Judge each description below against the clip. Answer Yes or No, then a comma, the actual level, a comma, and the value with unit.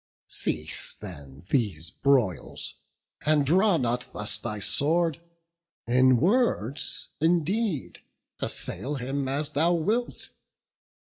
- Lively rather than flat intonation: Yes, wide, 6.2 semitones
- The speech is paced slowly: Yes, slow, 100 wpm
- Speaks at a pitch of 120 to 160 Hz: Yes, medium, 140 Hz